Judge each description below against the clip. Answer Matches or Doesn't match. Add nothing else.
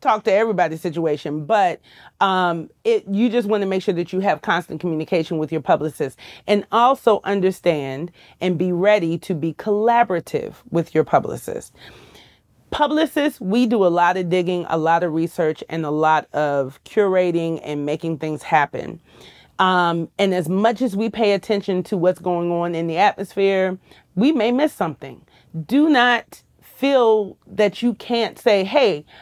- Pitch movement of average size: Matches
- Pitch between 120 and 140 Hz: Doesn't match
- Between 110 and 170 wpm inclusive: Matches